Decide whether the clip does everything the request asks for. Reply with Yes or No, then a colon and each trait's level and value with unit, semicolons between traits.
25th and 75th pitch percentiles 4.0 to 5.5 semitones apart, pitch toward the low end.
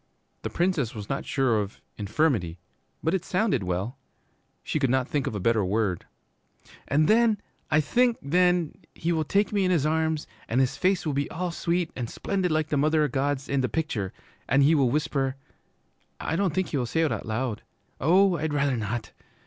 No: average, 5.2 semitones; medium, 145 Hz